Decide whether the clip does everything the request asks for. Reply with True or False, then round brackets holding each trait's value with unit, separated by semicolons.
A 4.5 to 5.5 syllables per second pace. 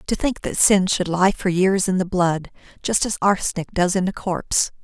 True (5.0 syllables/s)